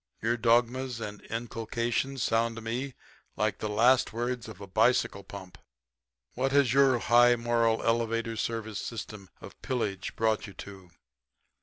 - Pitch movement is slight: Yes, narrow, 2.0 semitones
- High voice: No, low, 115 Hz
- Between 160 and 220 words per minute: No, average, 145 wpm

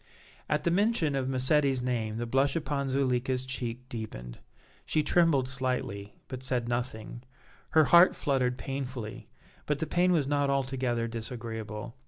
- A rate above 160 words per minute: No, average, 145 wpm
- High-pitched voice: No, low, 130 Hz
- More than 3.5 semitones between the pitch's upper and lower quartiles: No, average, 2.9 semitones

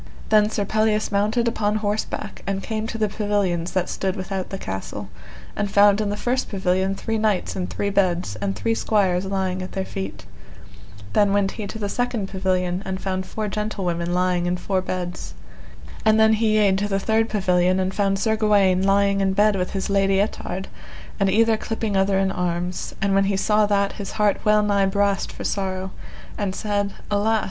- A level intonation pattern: Yes, narrow, 2.1 semitones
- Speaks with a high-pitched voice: Yes, high, 200 Hz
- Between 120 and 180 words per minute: No, average, 195 wpm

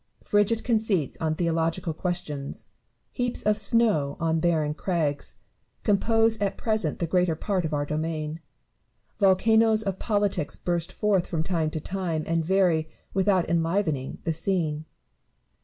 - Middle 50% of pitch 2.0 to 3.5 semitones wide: No, average, 4.3 semitones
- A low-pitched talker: No, medium, 175 Hz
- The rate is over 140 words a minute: No, slow, 135 wpm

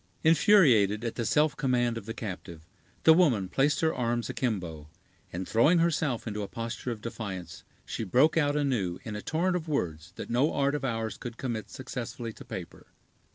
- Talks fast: No, average, 185 wpm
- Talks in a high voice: No, low, 120 Hz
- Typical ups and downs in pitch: No, wide, 5.7 semitones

